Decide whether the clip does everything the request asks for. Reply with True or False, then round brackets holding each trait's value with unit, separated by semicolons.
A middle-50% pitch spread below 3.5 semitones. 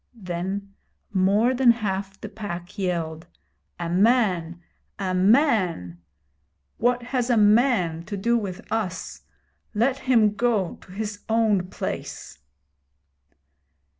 False (4.1 semitones)